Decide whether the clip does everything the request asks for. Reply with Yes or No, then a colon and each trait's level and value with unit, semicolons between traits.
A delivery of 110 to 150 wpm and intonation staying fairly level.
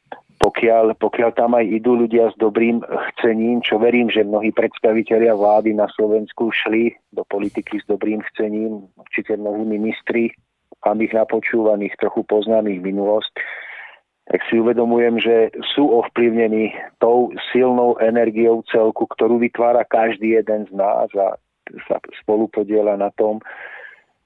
Yes: average, 130 wpm; narrow, 1.4 semitones